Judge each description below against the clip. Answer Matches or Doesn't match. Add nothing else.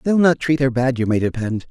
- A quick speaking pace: Matches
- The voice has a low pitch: Matches